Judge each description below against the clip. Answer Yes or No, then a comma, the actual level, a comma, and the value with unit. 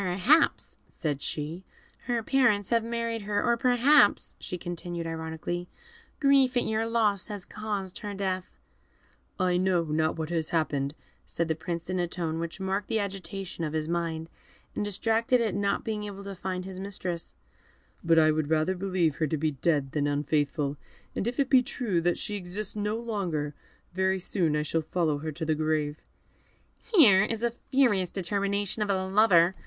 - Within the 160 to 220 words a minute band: Yes, average, 180 wpm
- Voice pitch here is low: No, medium, 185 Hz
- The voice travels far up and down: No, average, 4.6 semitones